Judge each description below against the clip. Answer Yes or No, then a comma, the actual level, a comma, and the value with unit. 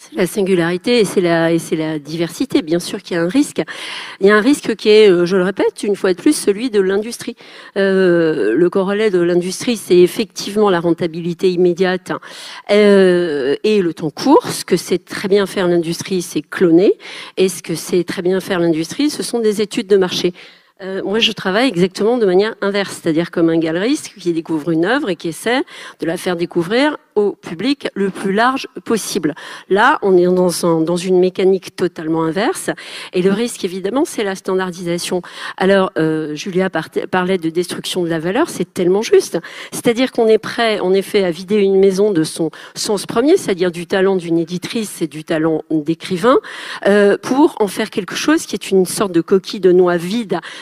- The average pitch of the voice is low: No, high, 190 Hz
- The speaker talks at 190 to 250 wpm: Yes, average, 200 wpm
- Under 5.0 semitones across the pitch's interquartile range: Yes, average, 3.6 semitones